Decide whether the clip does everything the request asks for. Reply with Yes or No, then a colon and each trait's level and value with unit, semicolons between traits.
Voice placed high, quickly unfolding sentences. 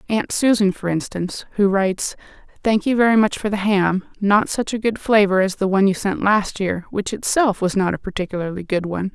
Yes: high, 200 Hz; fast, 215 wpm